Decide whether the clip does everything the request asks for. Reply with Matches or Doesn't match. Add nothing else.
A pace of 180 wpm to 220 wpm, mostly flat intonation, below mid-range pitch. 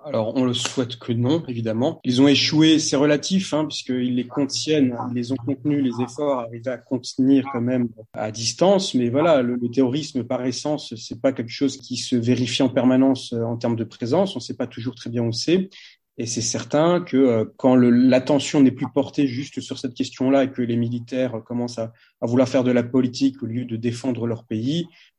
Matches